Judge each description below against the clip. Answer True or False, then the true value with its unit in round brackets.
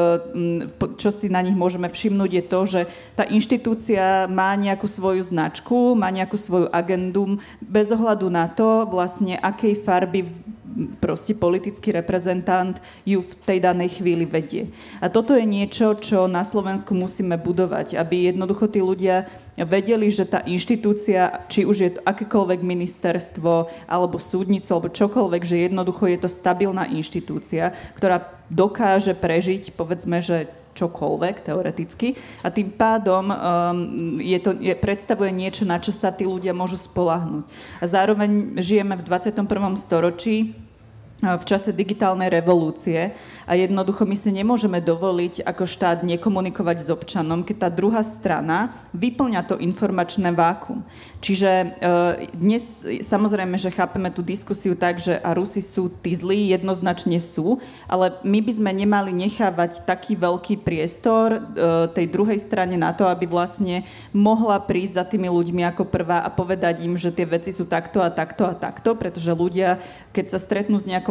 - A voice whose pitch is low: False (185 Hz)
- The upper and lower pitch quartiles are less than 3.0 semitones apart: True (2.6 semitones)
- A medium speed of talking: True (150 wpm)